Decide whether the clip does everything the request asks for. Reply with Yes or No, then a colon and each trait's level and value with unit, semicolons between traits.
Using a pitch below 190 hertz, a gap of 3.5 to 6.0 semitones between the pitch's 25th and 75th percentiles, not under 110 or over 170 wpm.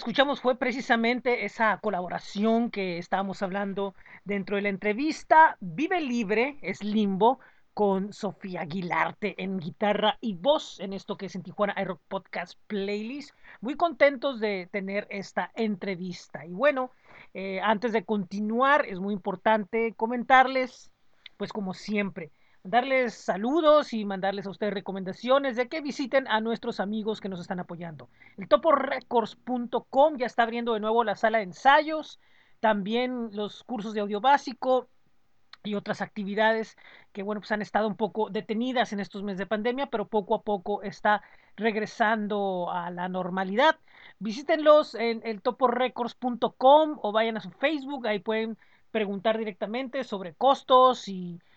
No: high, 220 Hz; average, 3.8 semitones; average, 150 wpm